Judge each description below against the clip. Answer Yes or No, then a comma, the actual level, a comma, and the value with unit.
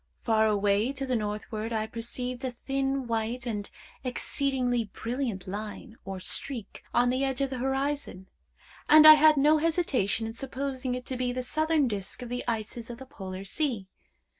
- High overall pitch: Yes, high, 245 Hz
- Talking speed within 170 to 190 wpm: Yes, average, 175 wpm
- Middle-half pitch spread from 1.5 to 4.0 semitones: Yes, average, 3.7 semitones